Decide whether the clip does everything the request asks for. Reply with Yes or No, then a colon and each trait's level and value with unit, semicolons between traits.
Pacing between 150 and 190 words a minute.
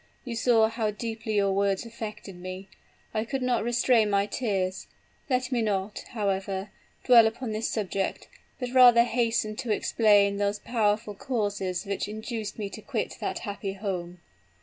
Yes: average, 155 wpm